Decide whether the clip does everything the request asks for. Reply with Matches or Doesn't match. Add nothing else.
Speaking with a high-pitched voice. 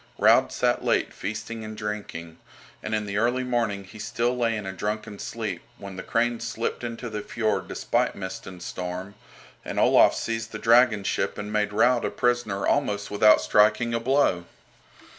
Doesn't match